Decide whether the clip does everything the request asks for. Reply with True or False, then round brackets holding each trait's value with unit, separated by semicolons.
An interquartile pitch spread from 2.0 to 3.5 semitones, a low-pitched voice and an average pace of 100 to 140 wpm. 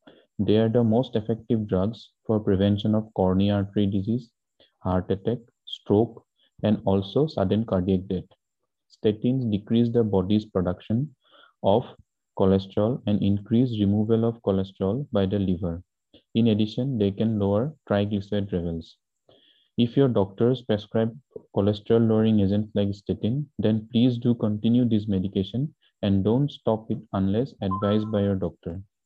True (2.7 semitones; 105 Hz; 135 wpm)